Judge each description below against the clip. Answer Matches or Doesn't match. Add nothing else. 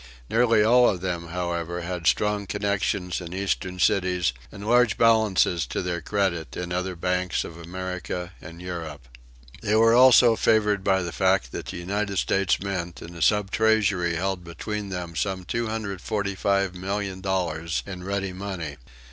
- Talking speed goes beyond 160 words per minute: Doesn't match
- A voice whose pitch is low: Matches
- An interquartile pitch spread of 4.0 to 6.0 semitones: Doesn't match